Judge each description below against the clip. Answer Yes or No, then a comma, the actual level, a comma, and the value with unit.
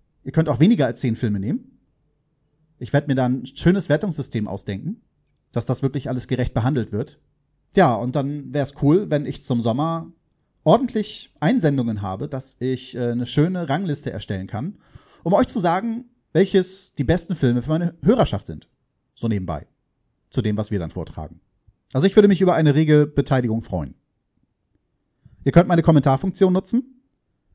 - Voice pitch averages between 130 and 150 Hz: Yes, medium, 140 Hz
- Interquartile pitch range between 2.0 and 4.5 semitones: No, wide, 5.6 semitones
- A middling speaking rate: Yes, average, 170 wpm